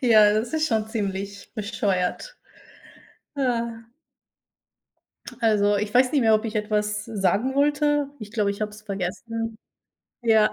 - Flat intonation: Yes, narrow, 2.2 semitones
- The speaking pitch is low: No, high, 215 Hz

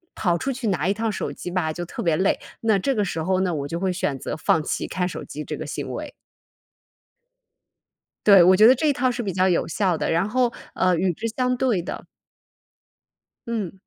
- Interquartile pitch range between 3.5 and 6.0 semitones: Yes, average, 4.6 semitones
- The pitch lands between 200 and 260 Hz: No, high, 190 Hz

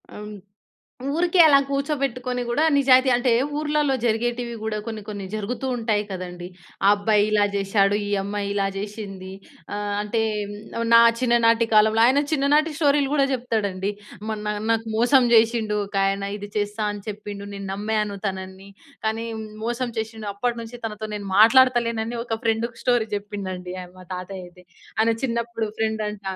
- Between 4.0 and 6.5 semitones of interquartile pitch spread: No, average, 3.0 semitones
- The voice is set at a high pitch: Yes, high, 220 Hz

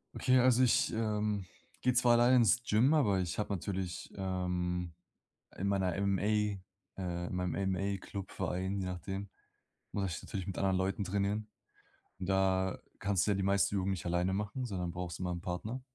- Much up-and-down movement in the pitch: No, narrow, 2.4 semitones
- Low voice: Yes, very low, 95 Hz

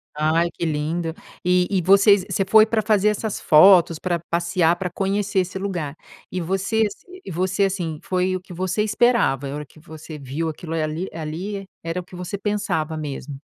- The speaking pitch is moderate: Yes, medium, 180 Hz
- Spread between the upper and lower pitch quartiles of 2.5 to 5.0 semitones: Yes, average, 3.7 semitones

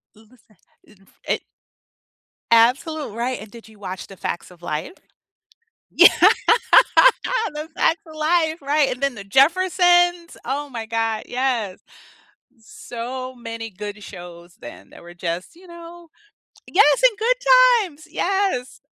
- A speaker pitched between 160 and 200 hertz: No, very high, 250 Hz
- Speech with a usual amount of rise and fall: No, wide, 7.6 semitones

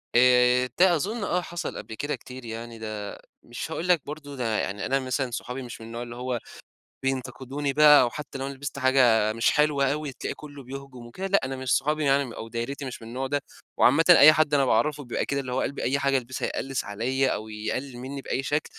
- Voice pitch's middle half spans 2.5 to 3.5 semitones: Yes, average, 2.9 semitones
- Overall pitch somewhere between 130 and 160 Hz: Yes, low, 135 Hz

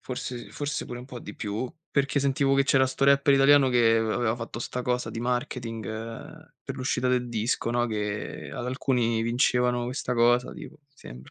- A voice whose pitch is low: Yes, low, 125 Hz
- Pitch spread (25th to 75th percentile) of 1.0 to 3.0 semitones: Yes, narrow, 2.4 semitones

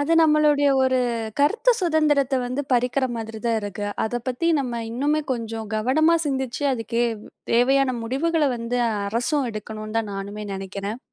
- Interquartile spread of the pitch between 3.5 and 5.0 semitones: Yes, average, 4.3 semitones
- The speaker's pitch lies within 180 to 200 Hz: No, very high, 250 Hz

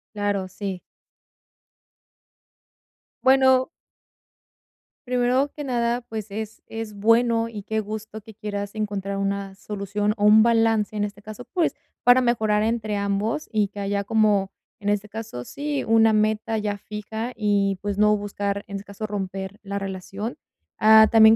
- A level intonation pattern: Yes, narrow, 1.9 semitones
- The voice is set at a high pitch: Yes, high, 210 Hz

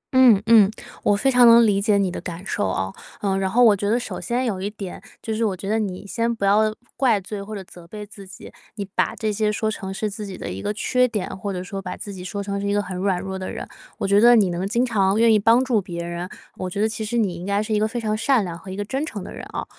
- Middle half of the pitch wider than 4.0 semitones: No, narrow, 2.6 semitones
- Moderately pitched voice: No, high, 205 Hz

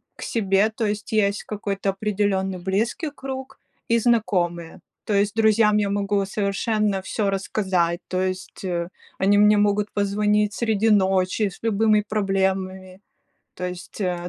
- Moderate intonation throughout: No, narrow, 1.9 semitones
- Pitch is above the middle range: Yes, high, 200 Hz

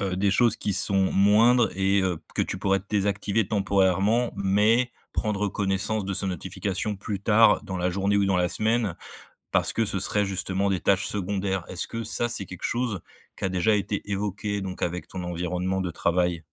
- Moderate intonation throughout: No, narrow, 1.9 semitones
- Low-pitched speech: Yes, low, 100 Hz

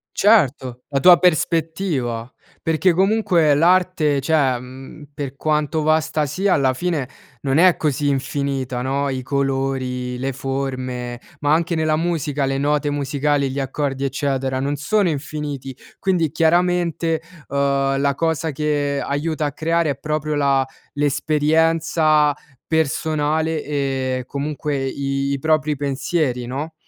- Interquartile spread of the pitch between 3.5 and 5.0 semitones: No, average, 2.8 semitones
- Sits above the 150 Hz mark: No, medium, 145 Hz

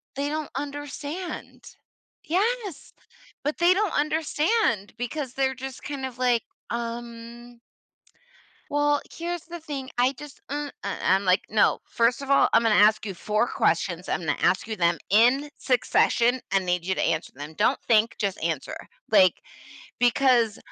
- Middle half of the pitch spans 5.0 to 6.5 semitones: Yes, wide, 5.6 semitones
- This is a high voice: Yes, high, 245 Hz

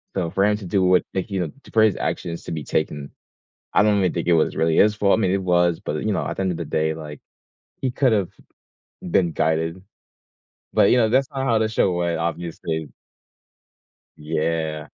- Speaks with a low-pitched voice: Yes, very low, 90 Hz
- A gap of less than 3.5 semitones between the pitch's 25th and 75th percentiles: No, average, 4.1 semitones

